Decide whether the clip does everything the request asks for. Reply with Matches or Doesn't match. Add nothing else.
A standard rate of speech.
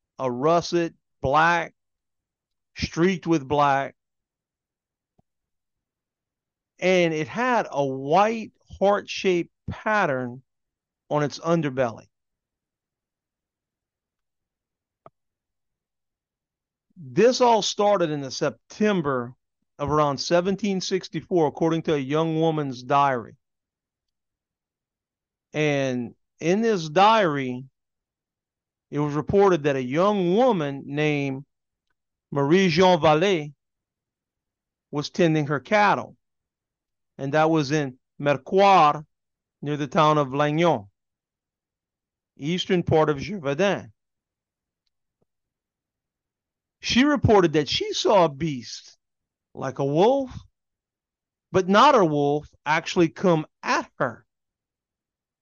Doesn't match